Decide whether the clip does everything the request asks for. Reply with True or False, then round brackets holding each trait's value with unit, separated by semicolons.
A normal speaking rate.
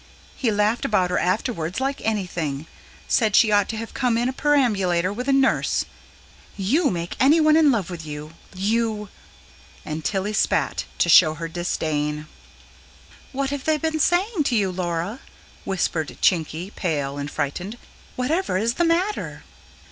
True (155 wpm)